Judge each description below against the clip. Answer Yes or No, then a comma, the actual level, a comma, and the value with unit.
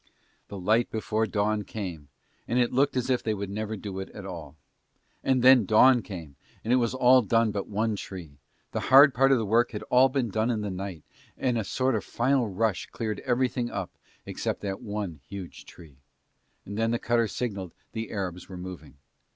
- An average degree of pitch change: Yes, average, 3.9 semitones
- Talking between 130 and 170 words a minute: No, average, 200 wpm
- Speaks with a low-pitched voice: Yes, low, 110 Hz